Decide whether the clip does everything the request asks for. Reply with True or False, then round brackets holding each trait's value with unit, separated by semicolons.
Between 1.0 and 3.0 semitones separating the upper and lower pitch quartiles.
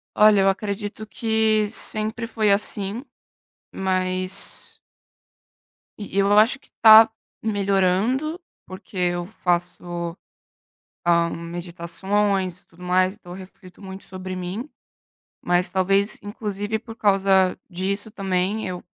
True (2.6 semitones)